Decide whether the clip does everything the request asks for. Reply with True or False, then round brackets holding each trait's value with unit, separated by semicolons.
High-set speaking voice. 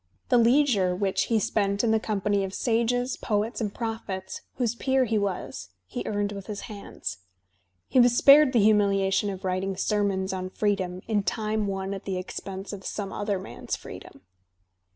True (205 Hz)